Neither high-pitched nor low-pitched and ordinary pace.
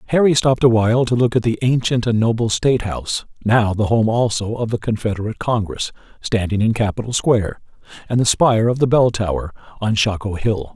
No: low, 115 Hz; average, 195 wpm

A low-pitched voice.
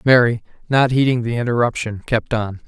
Yes: low, 120 Hz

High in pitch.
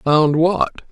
No: medium, 160 Hz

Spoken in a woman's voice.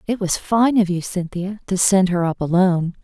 Yes: female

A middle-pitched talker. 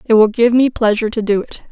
No: high, 225 Hz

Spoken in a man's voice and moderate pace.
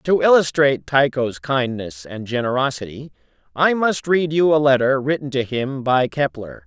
Yes: male; average, 155 wpm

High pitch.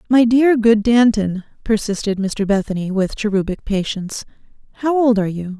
Yes: high, 215 Hz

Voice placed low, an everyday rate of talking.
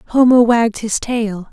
No: high, 225 Hz; average, 160 wpm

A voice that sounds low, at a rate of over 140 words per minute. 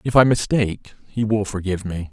Yes: low, 105 Hz; average, 200 wpm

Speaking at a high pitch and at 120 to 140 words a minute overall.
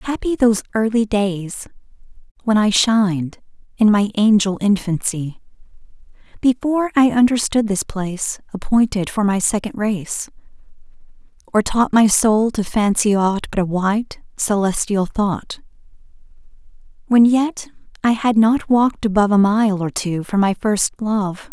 Yes: high, 210 Hz; slow, 135 wpm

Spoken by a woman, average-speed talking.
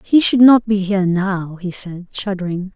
Yes: female; average, 195 wpm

